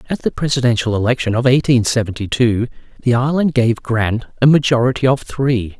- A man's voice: Yes, male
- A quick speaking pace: No, average, 165 wpm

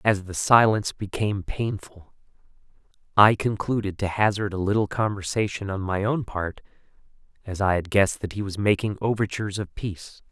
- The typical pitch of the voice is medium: No, low, 100 Hz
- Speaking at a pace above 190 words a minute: No, average, 155 wpm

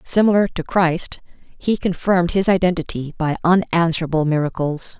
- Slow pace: Yes, slow, 120 wpm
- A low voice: No, medium, 170 Hz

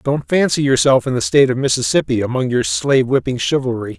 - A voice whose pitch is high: No, low, 135 Hz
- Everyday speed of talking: Yes, average, 180 wpm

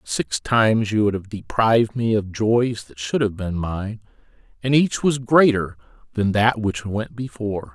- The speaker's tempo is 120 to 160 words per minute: No, average, 180 wpm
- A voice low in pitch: Yes, low, 110 Hz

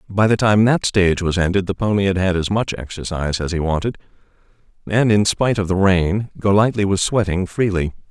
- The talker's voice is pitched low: Yes, very low, 95 Hz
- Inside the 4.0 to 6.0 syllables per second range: Yes, 5.7 syllables/s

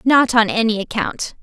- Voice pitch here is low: No, high, 230 Hz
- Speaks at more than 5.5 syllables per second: No, 4.7 syllables/s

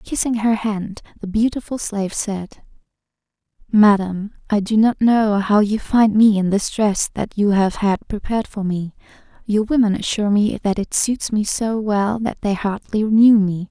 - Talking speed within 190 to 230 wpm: No, average, 180 wpm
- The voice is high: Yes, high, 210 Hz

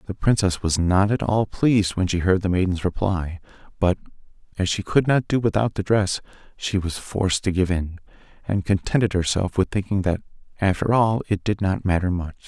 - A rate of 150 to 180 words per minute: No, average, 195 wpm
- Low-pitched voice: Yes, very low, 95 Hz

